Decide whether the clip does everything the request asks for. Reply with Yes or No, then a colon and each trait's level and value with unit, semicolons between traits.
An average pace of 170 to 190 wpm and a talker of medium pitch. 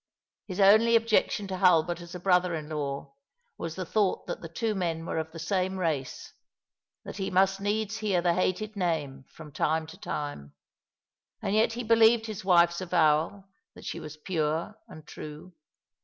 Yes: average, 180 wpm; medium, 180 Hz